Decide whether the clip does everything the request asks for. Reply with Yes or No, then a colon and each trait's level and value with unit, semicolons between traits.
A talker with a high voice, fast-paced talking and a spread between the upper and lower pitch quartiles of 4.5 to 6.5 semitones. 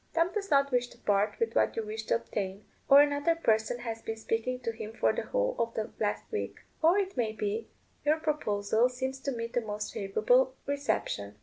Yes: high, 240 Hz; fast, 210 wpm; average, 5.1 semitones